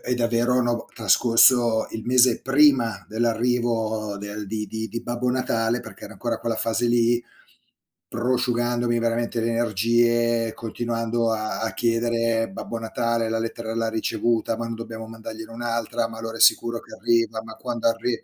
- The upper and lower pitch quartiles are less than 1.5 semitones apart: Yes, narrow, 1.0 semitones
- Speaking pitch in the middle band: No, low, 115 Hz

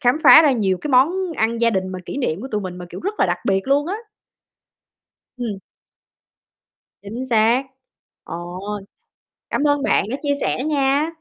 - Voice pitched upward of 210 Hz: Yes, very high, 250 Hz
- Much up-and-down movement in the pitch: Yes, wide, 6.4 semitones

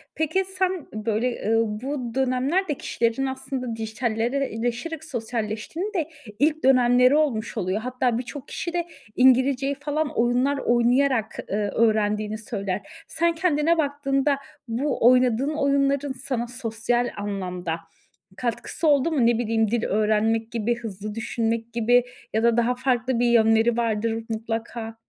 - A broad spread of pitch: No, average, 3.7 semitones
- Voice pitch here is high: Yes, high, 240 Hz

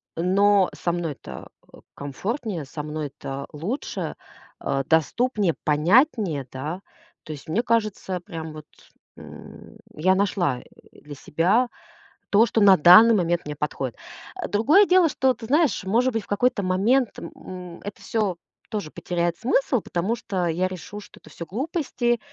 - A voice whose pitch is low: No, medium, 185 Hz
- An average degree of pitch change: No, wide, 6.0 semitones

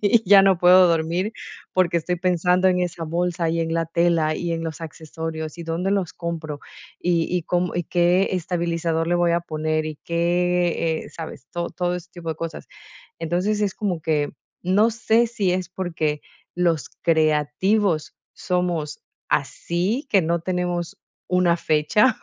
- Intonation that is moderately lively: No, narrow, 1.9 semitones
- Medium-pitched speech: Yes, medium, 175 Hz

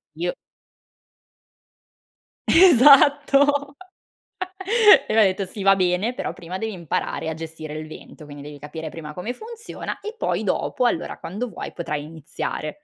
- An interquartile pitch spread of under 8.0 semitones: No, wide, 8.9 semitones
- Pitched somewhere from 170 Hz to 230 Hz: Yes, medium, 185 Hz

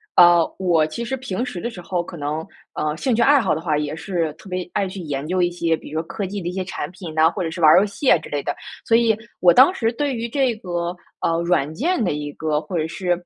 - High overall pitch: No, medium, 175 Hz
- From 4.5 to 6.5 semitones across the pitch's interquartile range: Yes, average, 5.1 semitones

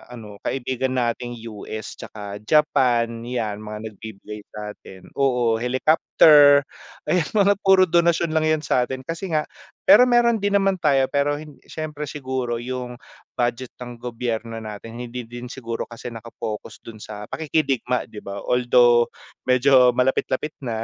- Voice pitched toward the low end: Yes, low, 125 Hz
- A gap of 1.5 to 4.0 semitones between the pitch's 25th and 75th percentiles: No, average, 4.5 semitones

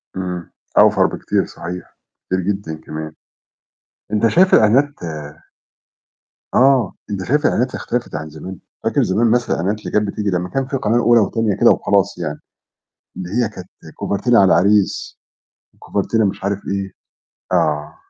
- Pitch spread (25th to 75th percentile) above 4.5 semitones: No, average, 4.1 semitones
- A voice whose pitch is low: Yes, low, 100 Hz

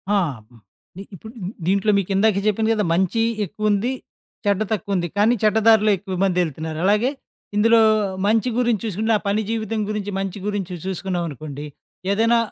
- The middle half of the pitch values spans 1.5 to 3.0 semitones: Yes, narrow, 2.6 semitones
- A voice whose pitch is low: No, high, 205 Hz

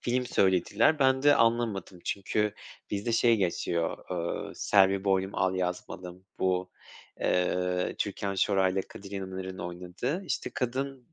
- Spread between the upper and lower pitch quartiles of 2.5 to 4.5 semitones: Yes, average, 4.2 semitones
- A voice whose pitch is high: No, very low, 95 Hz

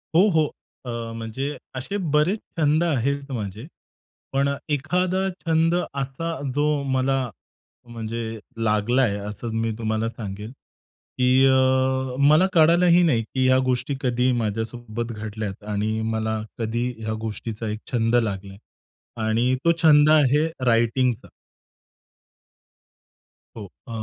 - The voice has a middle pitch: No, low, 120 Hz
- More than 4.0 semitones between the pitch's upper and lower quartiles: Yes, average, 4.8 semitones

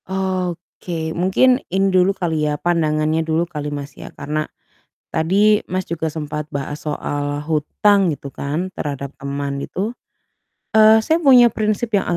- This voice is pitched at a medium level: Yes, medium, 165 Hz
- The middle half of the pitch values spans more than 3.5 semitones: Yes, average, 4.5 semitones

